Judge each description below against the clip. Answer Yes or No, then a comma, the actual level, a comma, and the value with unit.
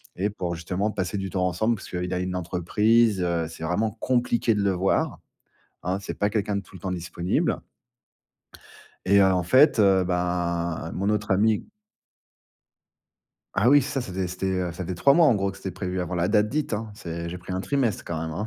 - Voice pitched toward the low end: Yes, very low, 95 Hz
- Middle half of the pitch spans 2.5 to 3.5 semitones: Yes, average, 3.0 semitones